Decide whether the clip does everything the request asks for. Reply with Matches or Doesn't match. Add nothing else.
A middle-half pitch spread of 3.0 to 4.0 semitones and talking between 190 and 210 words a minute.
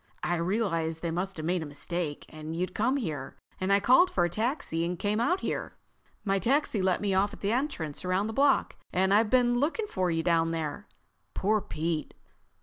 Doesn't match